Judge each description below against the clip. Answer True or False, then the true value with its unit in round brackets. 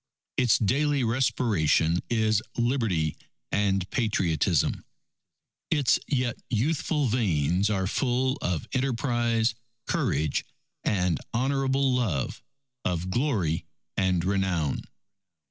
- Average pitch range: False (6.0 semitones)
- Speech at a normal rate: False (90 wpm)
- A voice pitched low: True (110 Hz)